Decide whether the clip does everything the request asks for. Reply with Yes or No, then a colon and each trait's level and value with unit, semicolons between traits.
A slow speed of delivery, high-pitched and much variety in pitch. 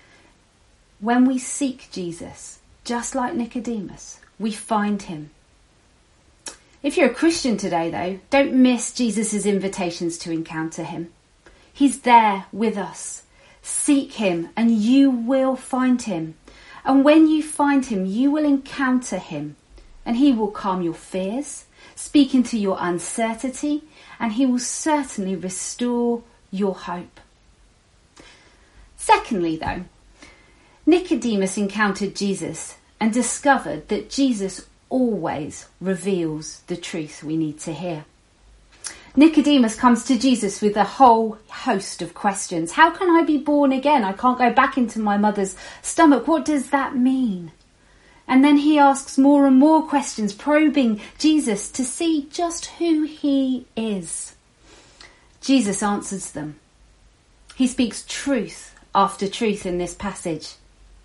Yes: slow, 130 wpm; high, 235 Hz; wide, 6.3 semitones